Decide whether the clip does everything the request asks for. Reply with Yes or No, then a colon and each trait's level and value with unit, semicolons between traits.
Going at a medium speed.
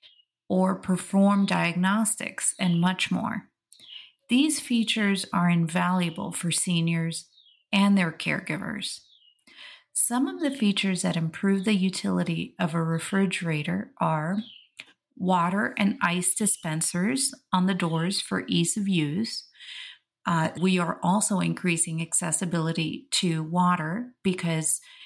No: slow, 115 wpm